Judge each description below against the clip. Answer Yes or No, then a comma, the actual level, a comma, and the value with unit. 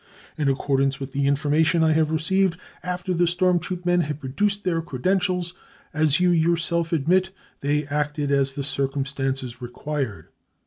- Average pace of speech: Yes, average, 160 wpm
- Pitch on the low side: No, medium, 155 Hz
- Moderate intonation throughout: Yes, average, 4.1 semitones